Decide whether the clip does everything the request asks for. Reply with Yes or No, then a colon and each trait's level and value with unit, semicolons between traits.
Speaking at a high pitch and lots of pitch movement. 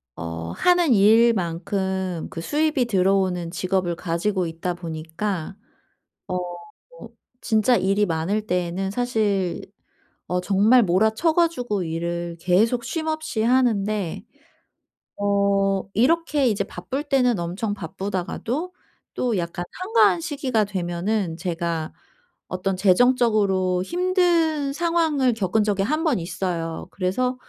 Yes: high, 200 Hz; wide, 5.8 semitones